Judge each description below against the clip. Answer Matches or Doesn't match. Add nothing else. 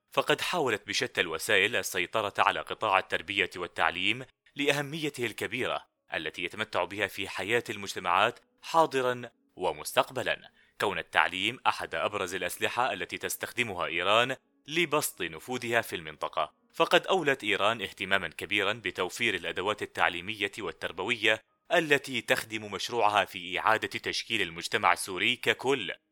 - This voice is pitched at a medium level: Doesn't match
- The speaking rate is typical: Matches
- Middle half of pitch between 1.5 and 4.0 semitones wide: Doesn't match